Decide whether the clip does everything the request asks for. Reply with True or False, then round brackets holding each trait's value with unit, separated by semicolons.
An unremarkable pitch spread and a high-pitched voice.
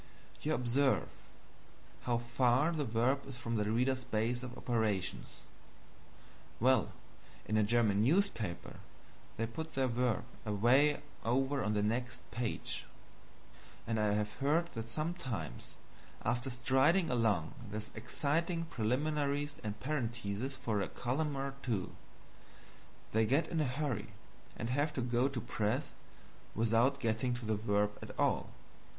False (4.0 semitones; 120 Hz)